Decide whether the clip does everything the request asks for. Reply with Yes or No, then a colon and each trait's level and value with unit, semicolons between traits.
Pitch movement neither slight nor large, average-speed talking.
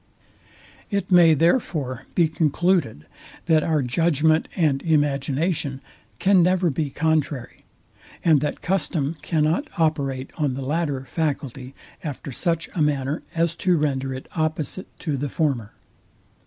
No: average, 3.4 semitones; slow, 130 wpm